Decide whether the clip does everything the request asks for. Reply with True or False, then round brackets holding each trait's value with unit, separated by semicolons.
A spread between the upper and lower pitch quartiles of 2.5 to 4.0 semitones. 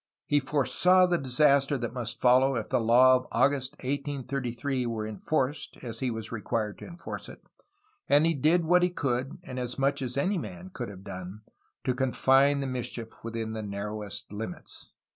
True (3.7 semitones)